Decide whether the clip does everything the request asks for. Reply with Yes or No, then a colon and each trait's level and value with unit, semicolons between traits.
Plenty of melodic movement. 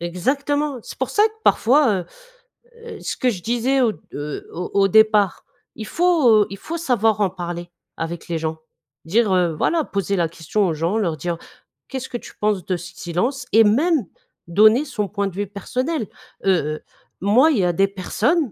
Yes: wide, 6.5 semitones